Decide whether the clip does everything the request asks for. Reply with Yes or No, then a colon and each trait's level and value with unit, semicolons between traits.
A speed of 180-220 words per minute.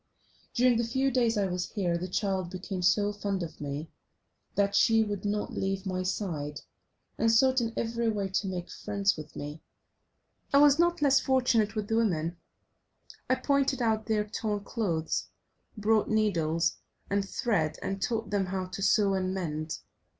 No: average, 170 wpm